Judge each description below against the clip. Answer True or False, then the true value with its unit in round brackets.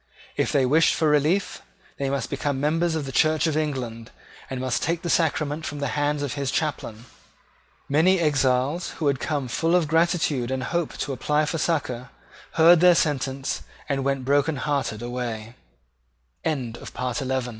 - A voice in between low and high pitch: True (145 Hz)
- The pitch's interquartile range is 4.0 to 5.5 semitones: False (3.3 semitones)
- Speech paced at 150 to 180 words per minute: True (155 wpm)